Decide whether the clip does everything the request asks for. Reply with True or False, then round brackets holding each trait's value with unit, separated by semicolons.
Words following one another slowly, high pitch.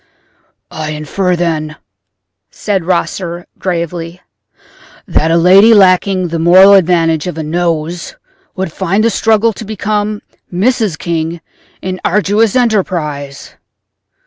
False (115 wpm; 180 Hz)